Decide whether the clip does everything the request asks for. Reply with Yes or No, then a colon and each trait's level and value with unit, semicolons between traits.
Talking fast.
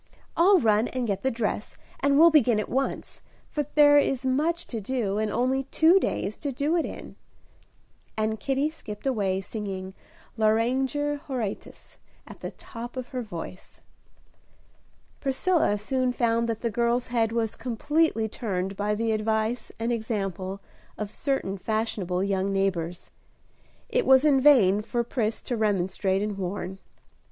No: average, 150 wpm